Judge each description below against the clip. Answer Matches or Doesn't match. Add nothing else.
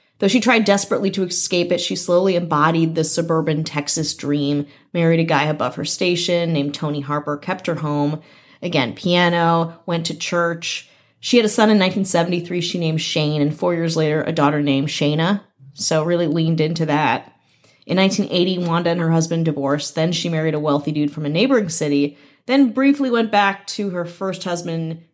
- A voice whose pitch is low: Doesn't match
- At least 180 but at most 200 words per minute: Matches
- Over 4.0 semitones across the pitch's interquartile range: Doesn't match